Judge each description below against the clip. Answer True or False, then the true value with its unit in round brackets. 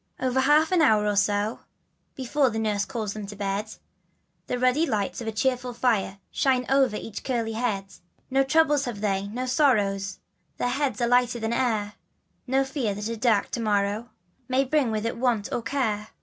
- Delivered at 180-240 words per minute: True (190 wpm)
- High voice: True (235 Hz)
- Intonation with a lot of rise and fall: False (3.8 semitones)